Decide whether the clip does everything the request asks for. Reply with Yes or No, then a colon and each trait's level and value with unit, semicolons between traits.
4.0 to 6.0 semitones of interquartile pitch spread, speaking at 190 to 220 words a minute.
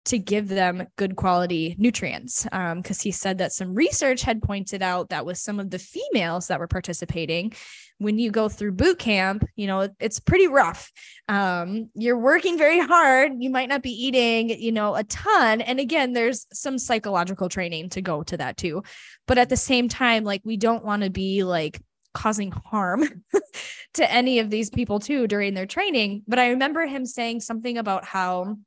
Yes: average, 4.7 semitones; average, 195 wpm